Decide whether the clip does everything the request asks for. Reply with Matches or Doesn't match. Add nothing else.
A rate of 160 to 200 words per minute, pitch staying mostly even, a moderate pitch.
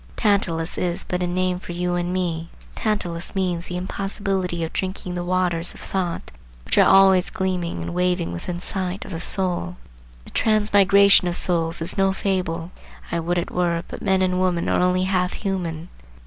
Matches